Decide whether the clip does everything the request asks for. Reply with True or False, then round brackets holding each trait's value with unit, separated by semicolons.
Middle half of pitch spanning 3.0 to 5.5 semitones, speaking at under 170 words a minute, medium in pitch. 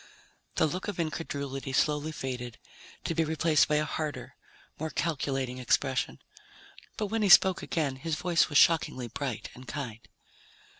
True (3.6 semitones; 150 wpm; 150 Hz)